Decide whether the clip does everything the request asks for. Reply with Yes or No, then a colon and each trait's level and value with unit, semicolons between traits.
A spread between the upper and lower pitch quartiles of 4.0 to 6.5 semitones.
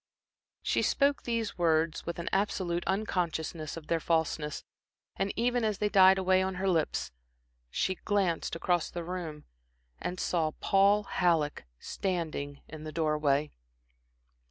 No: average, 3.4 semitones